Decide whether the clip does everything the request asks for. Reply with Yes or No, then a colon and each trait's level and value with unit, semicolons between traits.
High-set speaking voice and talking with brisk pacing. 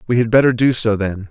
No: low, 115 Hz; fast, 275 wpm